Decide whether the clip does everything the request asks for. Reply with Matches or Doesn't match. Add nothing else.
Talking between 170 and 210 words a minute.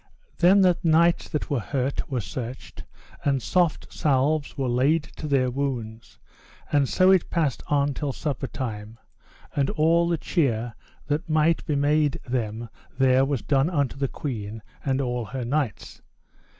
Doesn't match